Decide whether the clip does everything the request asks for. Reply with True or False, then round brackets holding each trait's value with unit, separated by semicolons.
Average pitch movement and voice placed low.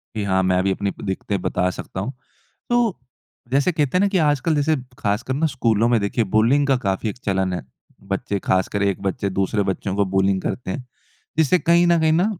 False (7.1 semitones; 105 Hz)